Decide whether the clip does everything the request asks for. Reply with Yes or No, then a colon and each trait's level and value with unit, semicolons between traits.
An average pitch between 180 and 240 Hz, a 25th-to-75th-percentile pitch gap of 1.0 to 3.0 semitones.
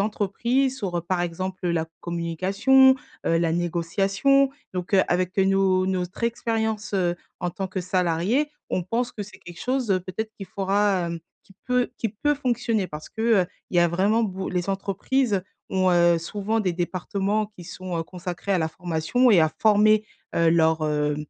No: high, 190 Hz; average, 3.7 semitones